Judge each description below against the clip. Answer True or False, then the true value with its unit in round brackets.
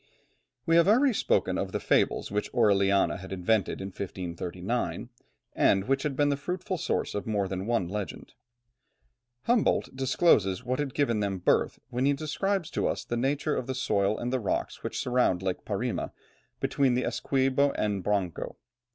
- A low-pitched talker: True (120 Hz)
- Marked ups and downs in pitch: True (6.2 semitones)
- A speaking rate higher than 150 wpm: True (175 wpm)